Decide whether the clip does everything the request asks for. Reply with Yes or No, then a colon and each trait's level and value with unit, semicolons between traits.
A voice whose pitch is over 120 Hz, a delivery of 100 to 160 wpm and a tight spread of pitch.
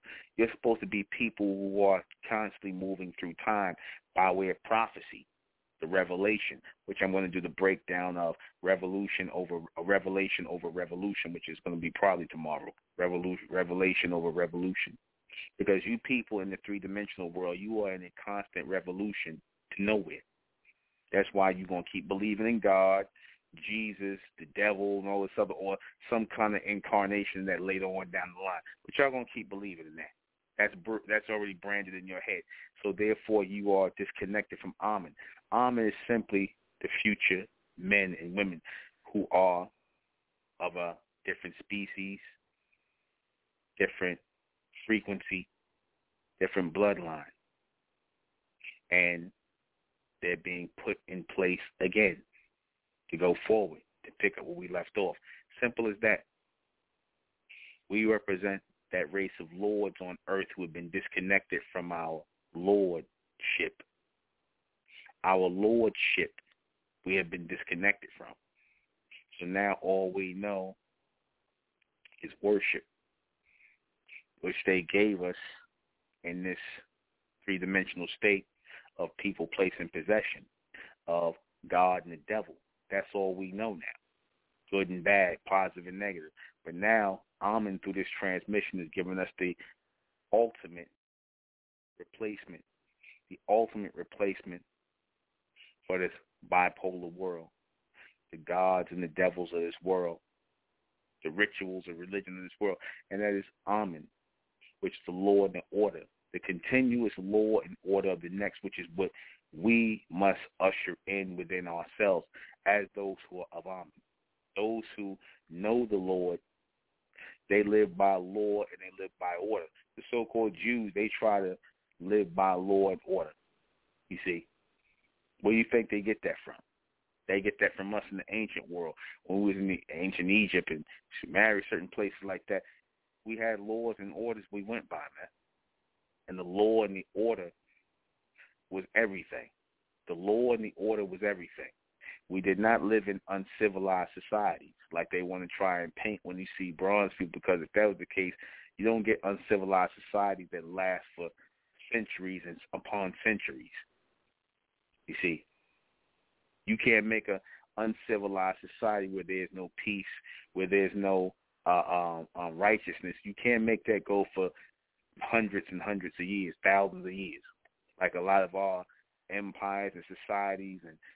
No: very low, 95 Hz; average, 150 wpm; narrow, 2.1 semitones